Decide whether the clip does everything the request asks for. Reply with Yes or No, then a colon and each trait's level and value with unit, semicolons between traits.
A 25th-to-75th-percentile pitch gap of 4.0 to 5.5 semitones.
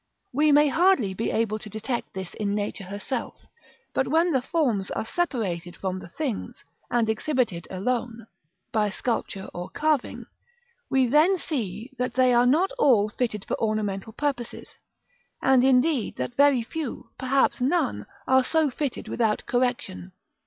Yes: average, 4.7 semitones